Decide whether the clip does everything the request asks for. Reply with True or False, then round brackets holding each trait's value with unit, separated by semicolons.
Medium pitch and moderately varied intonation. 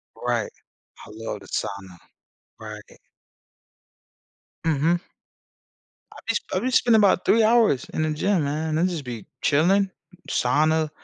False (155 Hz; 7.2 semitones)